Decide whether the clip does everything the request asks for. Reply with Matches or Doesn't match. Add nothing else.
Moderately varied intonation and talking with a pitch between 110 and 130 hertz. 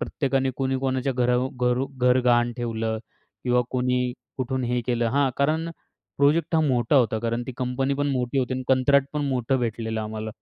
Doesn't match